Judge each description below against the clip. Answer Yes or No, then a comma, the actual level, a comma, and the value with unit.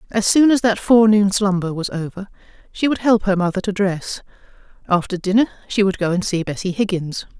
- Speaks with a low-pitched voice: No, high, 200 Hz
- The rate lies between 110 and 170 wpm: No, average, 195 wpm